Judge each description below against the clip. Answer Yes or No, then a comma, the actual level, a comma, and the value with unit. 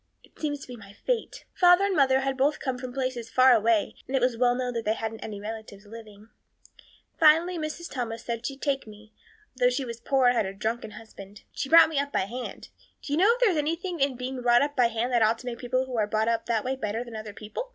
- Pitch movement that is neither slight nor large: Yes, average, 3.8 semitones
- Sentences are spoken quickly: Yes, fast, 255 wpm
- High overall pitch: Yes, high, 245 Hz